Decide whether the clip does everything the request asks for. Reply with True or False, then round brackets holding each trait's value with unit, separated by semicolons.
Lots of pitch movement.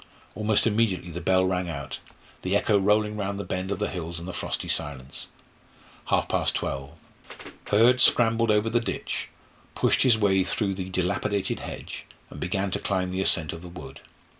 False (3.0 semitones)